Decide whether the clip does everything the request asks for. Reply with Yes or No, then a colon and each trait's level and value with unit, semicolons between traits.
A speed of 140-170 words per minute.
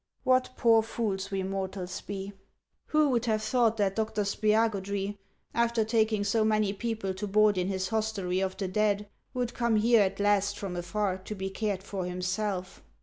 No: average, 180 wpm